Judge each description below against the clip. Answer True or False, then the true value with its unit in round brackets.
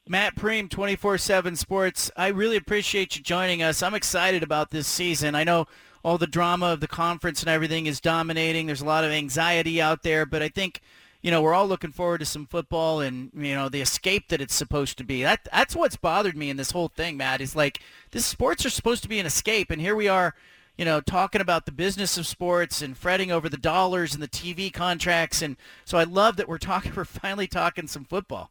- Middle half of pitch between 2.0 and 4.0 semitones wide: True (3.1 semitones)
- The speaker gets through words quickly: True (235 wpm)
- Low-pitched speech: False (170 Hz)